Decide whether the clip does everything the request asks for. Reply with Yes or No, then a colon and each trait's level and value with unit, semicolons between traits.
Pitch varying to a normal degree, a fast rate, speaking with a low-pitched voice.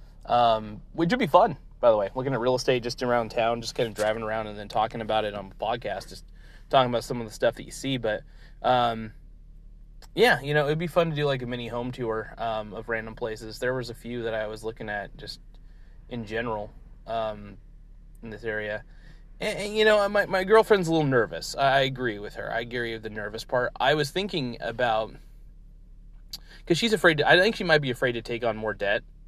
Yes: average, 3.9 semitones; fast, 230 wpm; low, 120 Hz